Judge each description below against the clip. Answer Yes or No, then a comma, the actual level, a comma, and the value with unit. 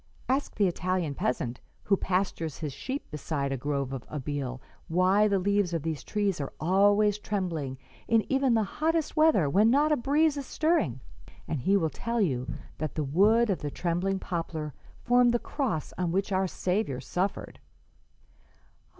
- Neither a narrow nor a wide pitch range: No, wide, 6.4 semitones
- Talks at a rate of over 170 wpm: No, average, 165 wpm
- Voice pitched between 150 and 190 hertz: Yes, medium, 185 Hz